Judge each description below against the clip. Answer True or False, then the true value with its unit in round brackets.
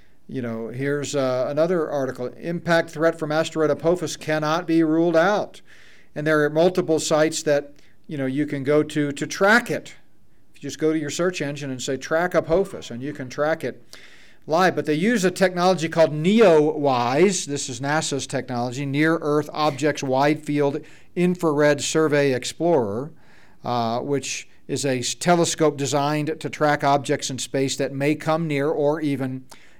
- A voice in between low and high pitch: True (150 Hz)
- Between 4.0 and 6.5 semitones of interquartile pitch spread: False (2.5 semitones)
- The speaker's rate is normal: True (170 wpm)